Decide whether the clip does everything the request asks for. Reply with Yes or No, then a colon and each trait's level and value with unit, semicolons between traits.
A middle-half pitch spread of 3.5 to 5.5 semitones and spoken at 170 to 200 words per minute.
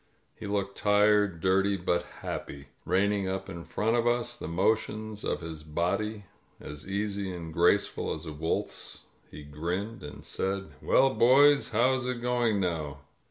No: average, 4.3 semitones; average, 160 wpm